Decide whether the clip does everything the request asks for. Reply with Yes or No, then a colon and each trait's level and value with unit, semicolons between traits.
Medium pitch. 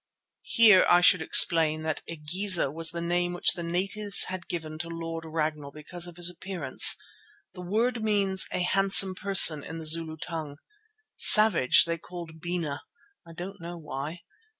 Yes: medium, 170 Hz